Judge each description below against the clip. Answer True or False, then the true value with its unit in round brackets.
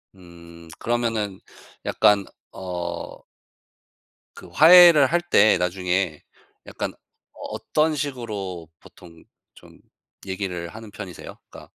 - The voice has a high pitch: False (100 Hz)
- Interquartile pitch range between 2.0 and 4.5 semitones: False (5.2 semitones)